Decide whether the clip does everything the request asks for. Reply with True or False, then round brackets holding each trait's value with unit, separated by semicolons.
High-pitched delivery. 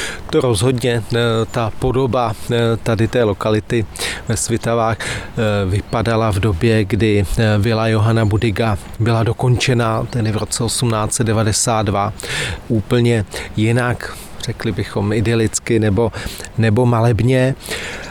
False (115 Hz)